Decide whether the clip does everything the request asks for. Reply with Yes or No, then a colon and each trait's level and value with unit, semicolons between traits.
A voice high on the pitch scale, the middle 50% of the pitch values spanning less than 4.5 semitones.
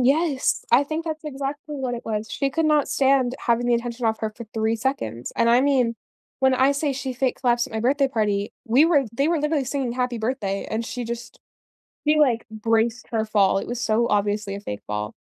Yes: high, 245 Hz; average, 3.8 semitones